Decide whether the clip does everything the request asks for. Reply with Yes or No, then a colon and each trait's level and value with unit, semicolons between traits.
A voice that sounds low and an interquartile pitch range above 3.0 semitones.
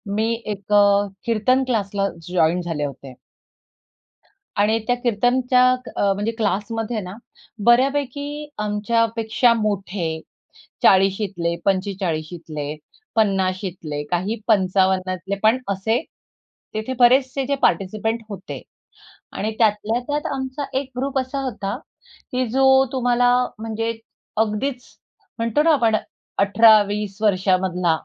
No: high, 210 Hz; average, 4.2 semitones